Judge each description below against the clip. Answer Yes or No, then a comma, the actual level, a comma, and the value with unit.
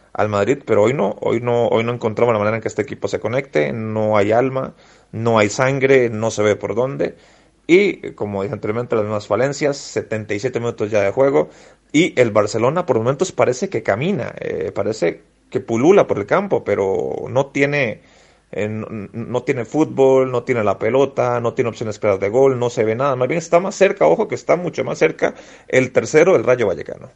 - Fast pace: Yes, fast, 210 wpm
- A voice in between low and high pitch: No, low, 120 Hz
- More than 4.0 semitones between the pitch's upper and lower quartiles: Yes, average, 4.8 semitones